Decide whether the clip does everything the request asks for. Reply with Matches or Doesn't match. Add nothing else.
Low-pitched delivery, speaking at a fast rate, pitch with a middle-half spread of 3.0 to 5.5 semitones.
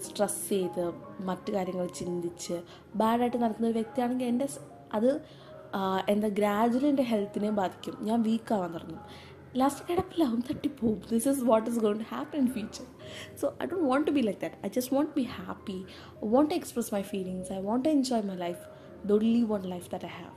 Doesn't match